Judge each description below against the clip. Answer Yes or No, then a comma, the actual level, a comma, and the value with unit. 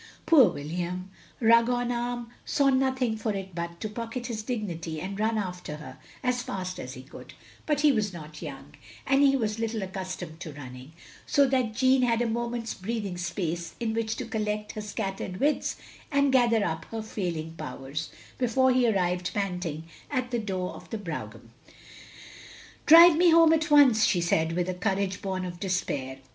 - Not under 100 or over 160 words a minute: No, average, 180 wpm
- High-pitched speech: Yes, high, 210 Hz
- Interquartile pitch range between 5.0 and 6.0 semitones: Yes, wide, 5.4 semitones